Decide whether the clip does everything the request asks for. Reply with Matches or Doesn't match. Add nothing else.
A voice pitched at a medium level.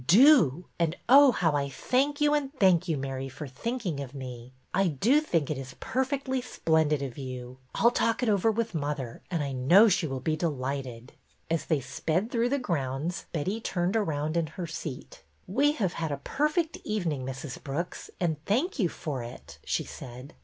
Matches